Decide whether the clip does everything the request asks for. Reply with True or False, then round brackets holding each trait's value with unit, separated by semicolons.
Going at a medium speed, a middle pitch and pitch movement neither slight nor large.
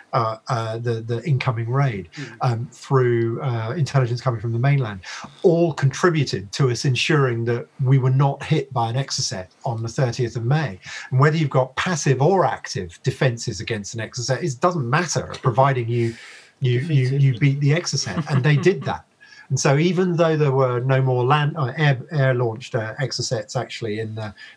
False (185 wpm; 130 Hz; 3.0 semitones)